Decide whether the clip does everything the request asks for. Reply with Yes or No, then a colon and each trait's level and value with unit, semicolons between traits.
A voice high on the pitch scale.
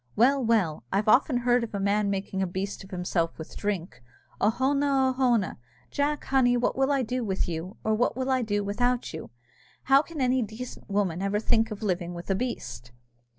Yes: high, 220 Hz